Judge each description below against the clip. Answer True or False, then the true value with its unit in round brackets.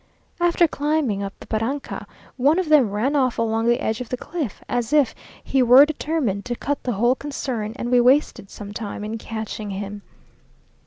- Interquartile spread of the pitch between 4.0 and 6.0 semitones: True (4.7 semitones)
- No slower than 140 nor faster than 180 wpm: False (190 wpm)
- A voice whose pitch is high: True (245 Hz)